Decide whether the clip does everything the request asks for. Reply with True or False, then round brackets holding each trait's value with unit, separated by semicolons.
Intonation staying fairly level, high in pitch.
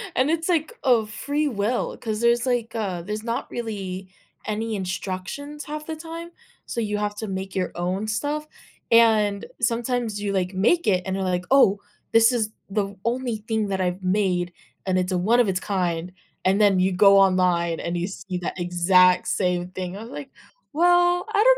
False (4.5 semitones; 205 Hz)